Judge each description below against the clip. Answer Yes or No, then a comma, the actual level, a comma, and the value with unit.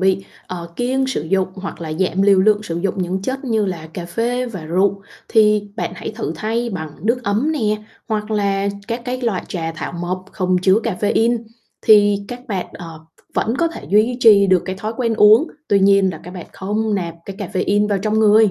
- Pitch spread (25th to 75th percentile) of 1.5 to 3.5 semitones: Yes, average, 3.1 semitones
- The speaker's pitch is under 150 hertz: No, high, 205 Hz